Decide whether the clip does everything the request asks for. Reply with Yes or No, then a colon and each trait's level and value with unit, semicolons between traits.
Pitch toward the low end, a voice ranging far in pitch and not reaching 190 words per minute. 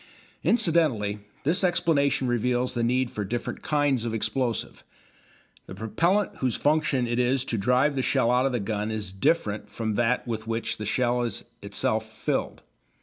No: low, 120 Hz; average, 3.5 semitones; average, 165 wpm